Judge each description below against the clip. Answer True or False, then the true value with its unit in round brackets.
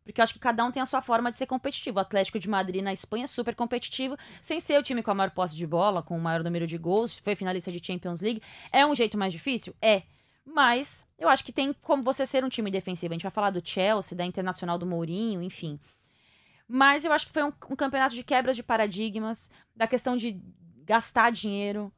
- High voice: True (220 Hz)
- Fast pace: True (240 wpm)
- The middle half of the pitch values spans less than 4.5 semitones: False (5.6 semitones)